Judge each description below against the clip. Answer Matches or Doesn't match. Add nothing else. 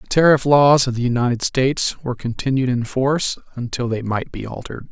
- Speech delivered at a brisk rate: Doesn't match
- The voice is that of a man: Matches